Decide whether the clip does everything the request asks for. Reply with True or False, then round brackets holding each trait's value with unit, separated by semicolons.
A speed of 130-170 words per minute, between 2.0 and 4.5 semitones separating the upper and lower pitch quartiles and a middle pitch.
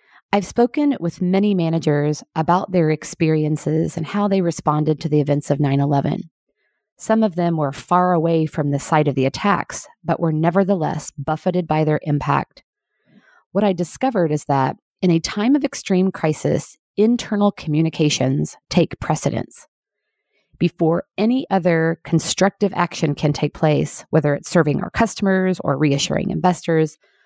True (150 wpm; 3.9 semitones; 165 Hz)